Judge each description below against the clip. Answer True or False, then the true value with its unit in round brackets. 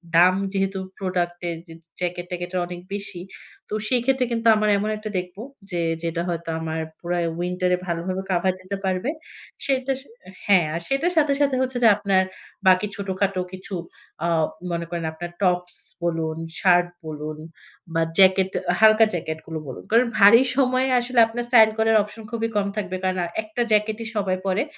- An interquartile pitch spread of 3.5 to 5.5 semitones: True (4.0 semitones)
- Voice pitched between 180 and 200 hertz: True (190 Hz)